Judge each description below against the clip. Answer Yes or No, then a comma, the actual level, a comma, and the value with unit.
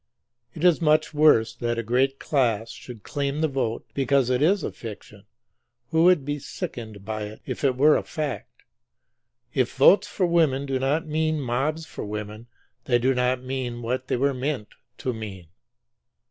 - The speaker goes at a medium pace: Yes, average, 180 wpm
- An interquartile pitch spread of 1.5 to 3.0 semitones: No, average, 4.3 semitones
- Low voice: Yes, low, 130 Hz